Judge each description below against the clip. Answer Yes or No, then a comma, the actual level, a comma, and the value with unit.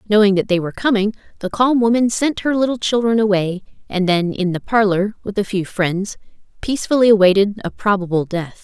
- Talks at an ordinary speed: Yes, average, 190 wpm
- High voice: Yes, high, 205 Hz